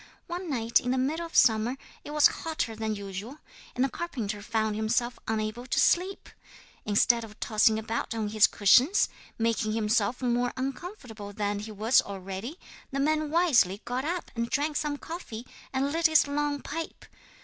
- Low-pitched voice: No, high, 240 Hz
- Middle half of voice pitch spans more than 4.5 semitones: Yes, average, 5.3 semitones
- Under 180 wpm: Yes, average, 170 wpm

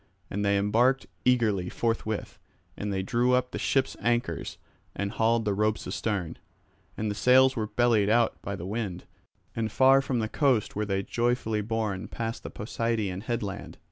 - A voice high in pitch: No, low, 110 Hz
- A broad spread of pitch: No, average, 2.9 semitones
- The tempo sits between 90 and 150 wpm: No, average, 170 wpm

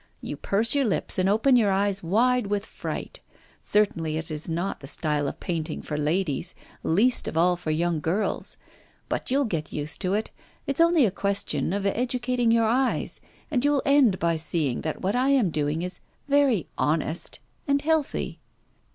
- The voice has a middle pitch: No, high, 195 Hz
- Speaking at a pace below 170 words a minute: No, average, 175 wpm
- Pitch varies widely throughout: Yes, wide, 7.3 semitones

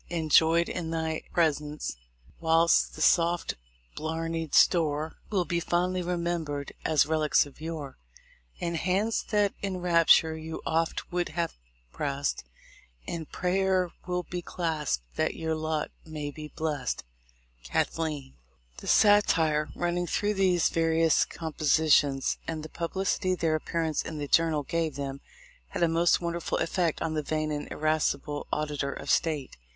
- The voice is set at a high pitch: No, medium, 160 Hz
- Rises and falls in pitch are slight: Yes, narrow, 2.2 semitones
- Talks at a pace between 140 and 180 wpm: Yes, average, 145 wpm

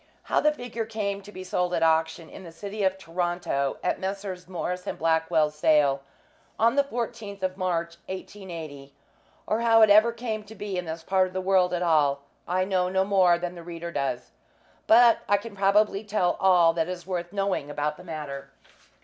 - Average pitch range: Yes, average, 3.5 semitones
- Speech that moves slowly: No, average, 195 wpm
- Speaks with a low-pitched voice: No, medium, 185 Hz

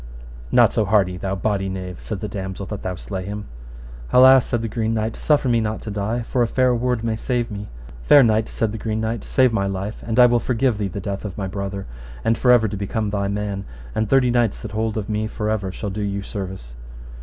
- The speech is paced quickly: Yes, fast, 240 wpm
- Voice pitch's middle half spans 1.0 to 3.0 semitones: Yes, narrow, 2.6 semitones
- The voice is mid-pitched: No, low, 105 Hz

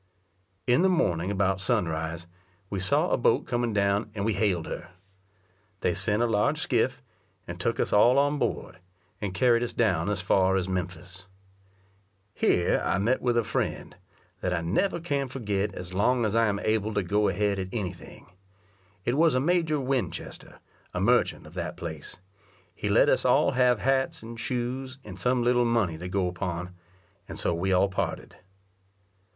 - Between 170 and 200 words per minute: Yes, average, 180 wpm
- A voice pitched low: Yes, low, 105 Hz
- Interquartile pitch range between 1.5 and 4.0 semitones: No, average, 5.0 semitones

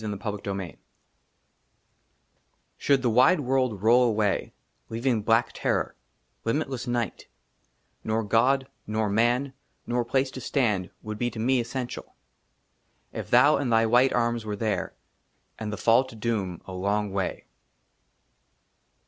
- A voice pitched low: Yes, low, 115 Hz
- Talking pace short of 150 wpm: Yes, average, 140 wpm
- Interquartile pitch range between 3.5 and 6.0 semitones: No, average, 3.1 semitones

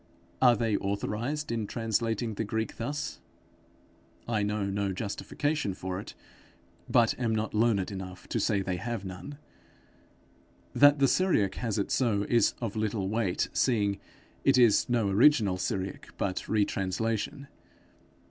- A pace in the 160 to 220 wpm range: No, average, 140 wpm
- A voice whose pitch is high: No, low, 110 Hz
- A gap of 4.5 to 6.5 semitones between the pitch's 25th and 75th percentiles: No, average, 3.2 semitones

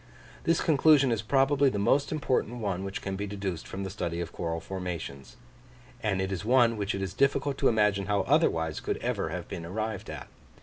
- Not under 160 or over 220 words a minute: Yes, fast, 205 wpm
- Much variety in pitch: Yes, wide, 5.8 semitones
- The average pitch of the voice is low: Yes, low, 100 Hz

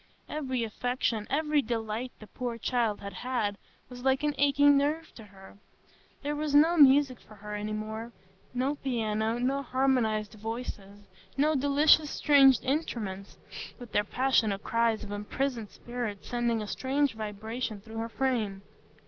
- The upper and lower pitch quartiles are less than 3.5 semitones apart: No, average, 4.1 semitones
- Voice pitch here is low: No, high, 240 Hz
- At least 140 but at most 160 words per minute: Yes, average, 145 wpm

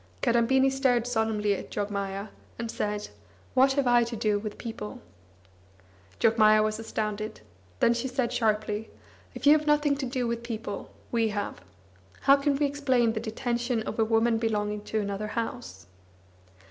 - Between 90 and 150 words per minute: No, average, 160 wpm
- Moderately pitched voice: No, high, 225 Hz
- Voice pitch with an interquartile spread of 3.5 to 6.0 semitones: No, average, 2.7 semitones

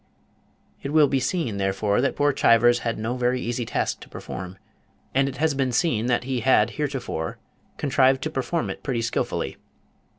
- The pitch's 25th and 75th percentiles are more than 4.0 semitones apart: No, average, 3.2 semitones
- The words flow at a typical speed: Yes, average, 175 wpm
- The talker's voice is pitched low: Yes, low, 125 Hz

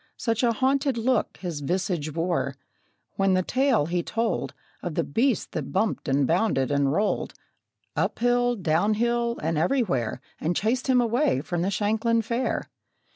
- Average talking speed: Yes, average, 160 wpm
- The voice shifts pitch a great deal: Yes, wide, 6.3 semitones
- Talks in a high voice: Yes, high, 210 Hz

